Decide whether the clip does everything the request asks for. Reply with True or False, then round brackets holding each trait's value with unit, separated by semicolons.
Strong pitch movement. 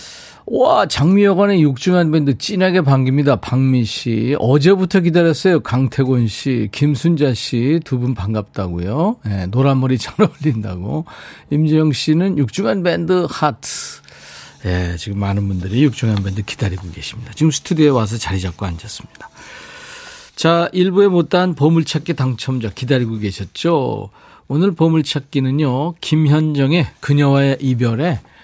True (6.4 semitones)